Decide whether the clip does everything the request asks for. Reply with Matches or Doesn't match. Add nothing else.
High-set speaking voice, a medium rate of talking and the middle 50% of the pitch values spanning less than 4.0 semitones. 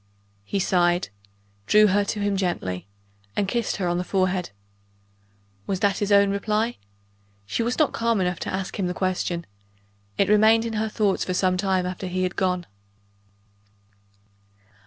Matches